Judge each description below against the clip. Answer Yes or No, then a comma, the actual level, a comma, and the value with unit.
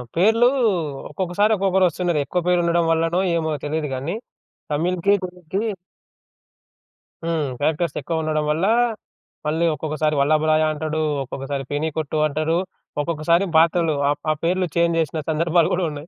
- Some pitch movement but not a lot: No, narrow, 2.3 semitones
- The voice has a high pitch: No, medium, 160 Hz